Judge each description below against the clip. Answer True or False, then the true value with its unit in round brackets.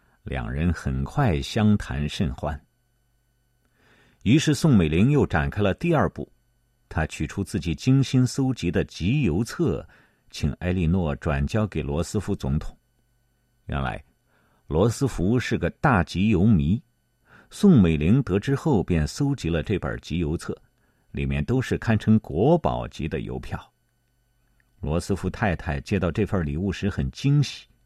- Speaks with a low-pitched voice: True (100 Hz)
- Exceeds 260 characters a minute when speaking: False (210 characters per minute)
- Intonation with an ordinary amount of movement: False (8.0 semitones)